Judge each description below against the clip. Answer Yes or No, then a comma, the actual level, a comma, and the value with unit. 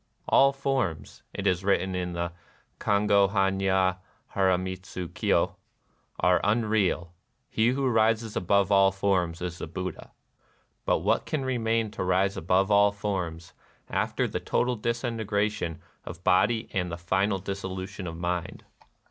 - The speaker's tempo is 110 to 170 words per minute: Yes, average, 140 wpm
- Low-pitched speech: Yes, very low, 95 Hz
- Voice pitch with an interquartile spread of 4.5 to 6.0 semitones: No, average, 2.9 semitones